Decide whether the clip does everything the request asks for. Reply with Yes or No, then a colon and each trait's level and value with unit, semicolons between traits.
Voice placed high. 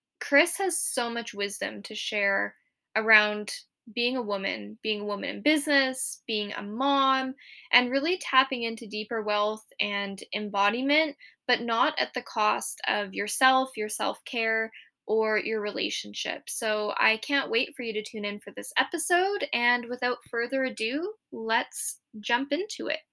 Yes: high, 230 Hz